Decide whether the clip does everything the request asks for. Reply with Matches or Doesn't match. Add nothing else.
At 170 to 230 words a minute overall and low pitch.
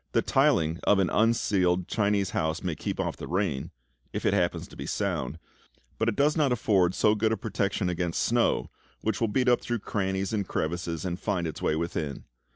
Matches